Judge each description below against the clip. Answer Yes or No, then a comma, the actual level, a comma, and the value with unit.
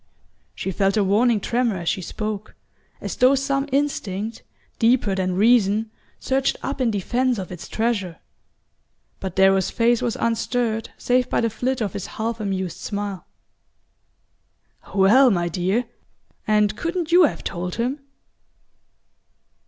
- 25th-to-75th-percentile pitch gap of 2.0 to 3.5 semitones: No, average, 4.4 semitones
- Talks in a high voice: Yes, high, 220 Hz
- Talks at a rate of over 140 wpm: No, slow, 135 wpm